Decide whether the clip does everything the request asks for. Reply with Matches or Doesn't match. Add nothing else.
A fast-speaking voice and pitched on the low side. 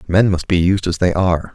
Matches